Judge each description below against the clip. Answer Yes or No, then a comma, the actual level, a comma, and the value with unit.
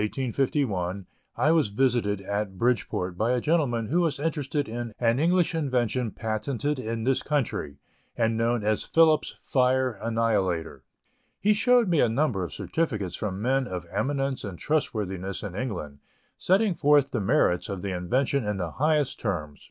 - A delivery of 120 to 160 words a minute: No, average, 170 wpm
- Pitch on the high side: No, low, 120 Hz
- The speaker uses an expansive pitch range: Yes, wide, 6.0 semitones